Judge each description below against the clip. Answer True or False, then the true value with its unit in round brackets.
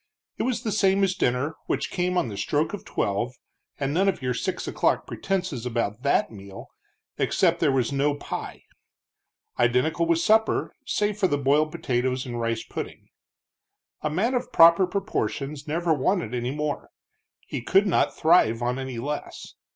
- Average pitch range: False (6.4 semitones)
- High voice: False (145 Hz)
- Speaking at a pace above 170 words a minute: False (165 wpm)